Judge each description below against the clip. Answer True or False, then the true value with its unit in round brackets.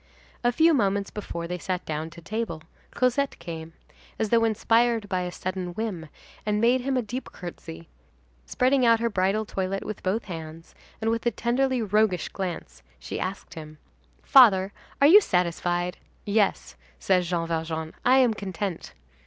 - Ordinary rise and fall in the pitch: True (4.9 semitones)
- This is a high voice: True (200 Hz)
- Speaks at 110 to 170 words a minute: True (160 wpm)